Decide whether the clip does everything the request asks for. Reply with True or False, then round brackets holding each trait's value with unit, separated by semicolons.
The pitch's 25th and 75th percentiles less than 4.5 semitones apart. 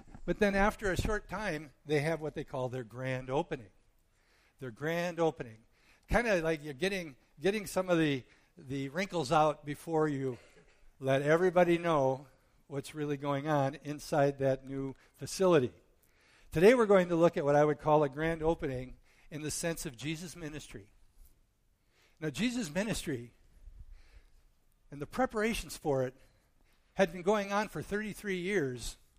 False (4.9 semitones)